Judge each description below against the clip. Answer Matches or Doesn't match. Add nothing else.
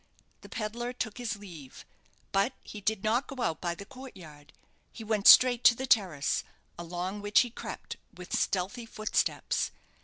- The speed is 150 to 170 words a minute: Matches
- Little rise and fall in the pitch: Doesn't match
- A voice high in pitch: Matches